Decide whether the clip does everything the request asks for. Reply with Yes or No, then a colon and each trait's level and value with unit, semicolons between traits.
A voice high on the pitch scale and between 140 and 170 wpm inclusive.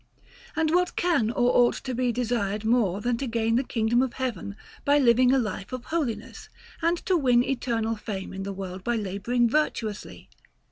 No: high, 240 Hz; average, 185 wpm